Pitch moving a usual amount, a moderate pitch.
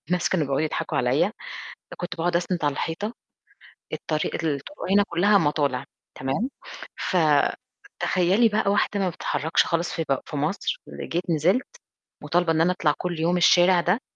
Yes: average, 3.2 semitones; medium, 175 Hz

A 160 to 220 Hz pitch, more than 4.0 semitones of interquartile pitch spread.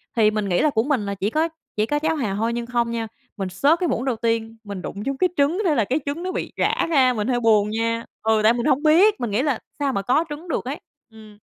No: high, 235 Hz; average, 5.2 semitones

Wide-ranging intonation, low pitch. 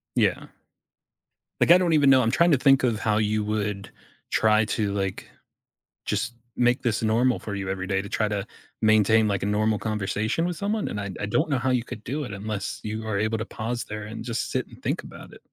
No: average, 2.9 semitones; low, 110 Hz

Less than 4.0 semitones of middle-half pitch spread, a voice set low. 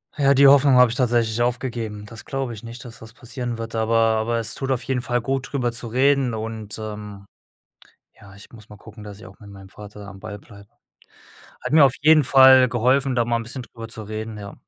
Yes: average, 2.9 semitones; low, 115 Hz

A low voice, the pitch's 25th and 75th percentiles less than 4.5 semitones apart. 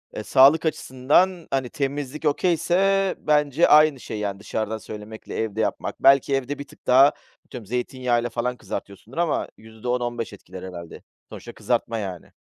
No: low, 125 Hz; average, 5.0 semitones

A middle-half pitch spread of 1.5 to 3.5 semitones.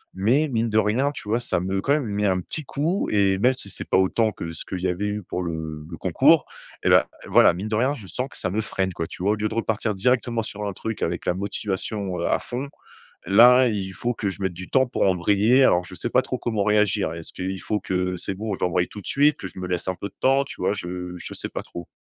No: average, 4.0 semitones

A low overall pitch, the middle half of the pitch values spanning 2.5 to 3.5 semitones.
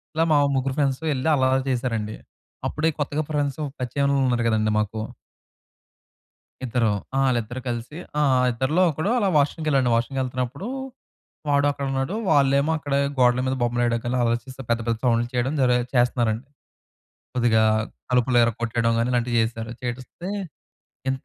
Yes: low, 125 Hz; average, 2.9 semitones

